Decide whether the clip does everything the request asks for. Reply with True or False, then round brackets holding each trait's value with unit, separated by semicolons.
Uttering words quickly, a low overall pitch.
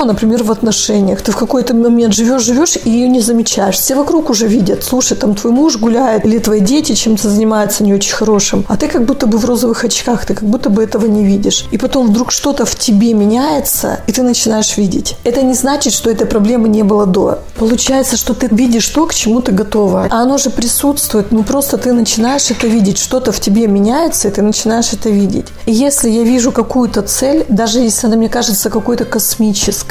False (210 wpm; 230 Hz)